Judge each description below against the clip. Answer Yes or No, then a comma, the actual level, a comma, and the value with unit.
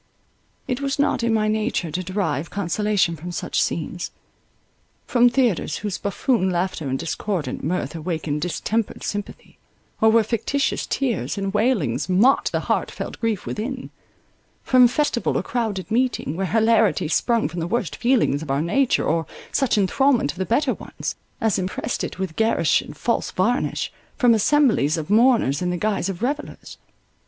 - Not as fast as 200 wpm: Yes, average, 165 wpm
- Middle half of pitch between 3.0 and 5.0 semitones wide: No, wide, 5.4 semitones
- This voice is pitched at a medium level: No, high, 210 Hz